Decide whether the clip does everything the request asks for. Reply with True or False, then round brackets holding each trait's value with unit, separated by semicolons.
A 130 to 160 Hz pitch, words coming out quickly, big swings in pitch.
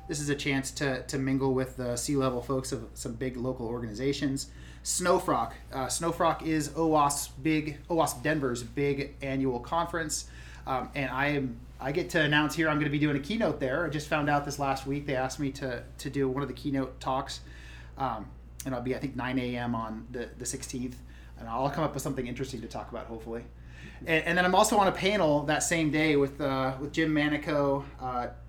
False (135 Hz; 215 wpm; 3.1 semitones)